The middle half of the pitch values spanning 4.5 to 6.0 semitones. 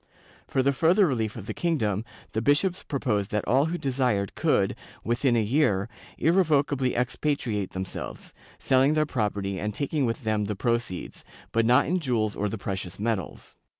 Yes: average, 5.3 semitones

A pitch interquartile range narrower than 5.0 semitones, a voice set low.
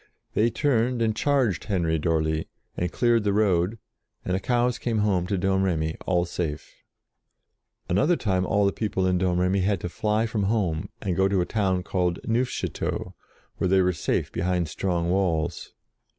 Yes: average, 3.4 semitones; very low, 95 Hz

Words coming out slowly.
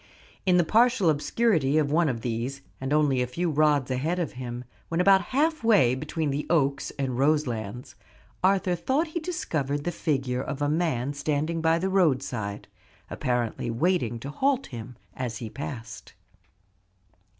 No: average, 160 wpm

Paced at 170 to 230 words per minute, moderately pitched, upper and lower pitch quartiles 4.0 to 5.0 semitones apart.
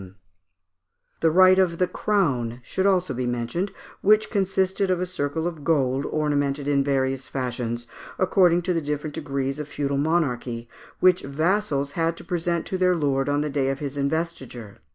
Yes: average, 175 wpm; medium, 150 Hz; average, 4.7 semitones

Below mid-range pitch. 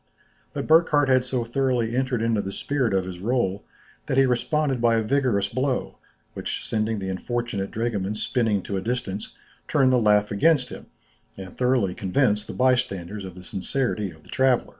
Yes: low, 115 Hz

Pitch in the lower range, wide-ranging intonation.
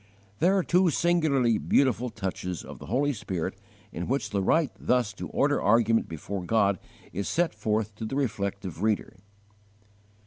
Yes: low, 110 Hz; wide, 5.8 semitones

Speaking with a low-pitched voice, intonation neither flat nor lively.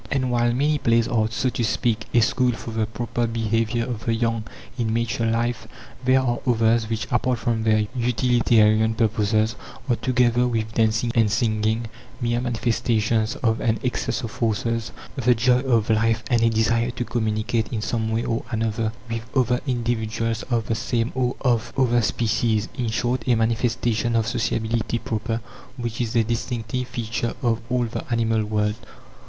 No: low, 115 Hz; narrow, 1.4 semitones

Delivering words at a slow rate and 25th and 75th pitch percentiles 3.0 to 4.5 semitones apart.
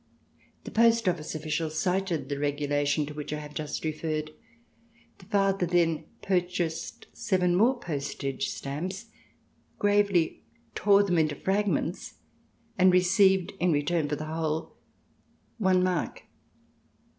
Yes: slow, 120 wpm; average, 4.0 semitones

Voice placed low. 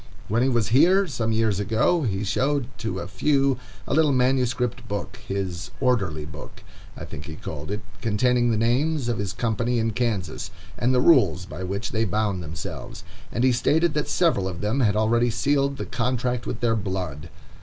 Yes: low, 115 Hz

